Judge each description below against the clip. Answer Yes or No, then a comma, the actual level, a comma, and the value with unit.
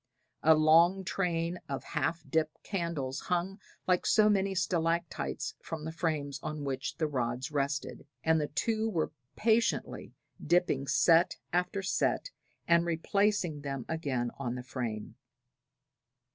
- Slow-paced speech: Yes, slow, 130 wpm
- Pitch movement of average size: Yes, average, 4.2 semitones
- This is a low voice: No, medium, 160 Hz